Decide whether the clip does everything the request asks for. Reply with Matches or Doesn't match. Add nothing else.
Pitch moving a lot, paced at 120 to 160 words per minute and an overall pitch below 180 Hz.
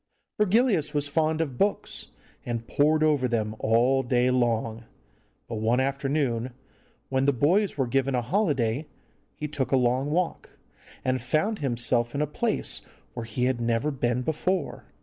Doesn't match